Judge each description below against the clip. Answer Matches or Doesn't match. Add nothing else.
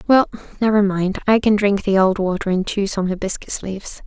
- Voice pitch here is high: Matches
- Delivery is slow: Doesn't match